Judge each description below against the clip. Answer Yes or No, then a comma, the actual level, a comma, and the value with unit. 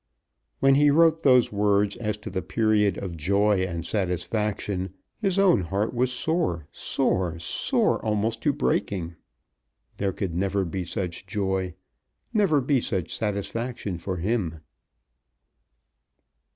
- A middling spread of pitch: Yes, average, 4.5 semitones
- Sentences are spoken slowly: Yes, slow, 125 wpm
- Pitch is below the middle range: Yes, low, 100 Hz